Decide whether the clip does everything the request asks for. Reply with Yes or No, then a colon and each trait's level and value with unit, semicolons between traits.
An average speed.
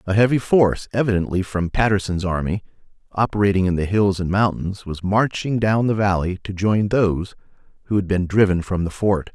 Yes: average, 180 wpm